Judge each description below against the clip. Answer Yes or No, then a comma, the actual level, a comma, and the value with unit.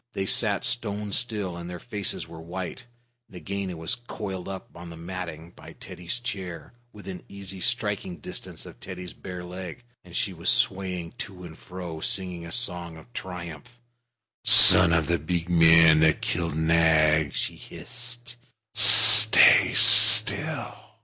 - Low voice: Yes, very low, 90 Hz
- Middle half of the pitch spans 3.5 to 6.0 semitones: No, average, 2.9 semitones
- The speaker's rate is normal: Yes, average, 145 wpm